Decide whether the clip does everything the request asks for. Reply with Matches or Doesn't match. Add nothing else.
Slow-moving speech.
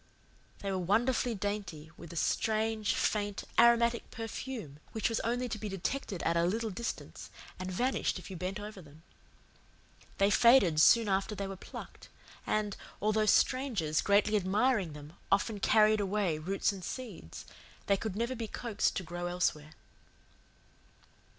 Doesn't match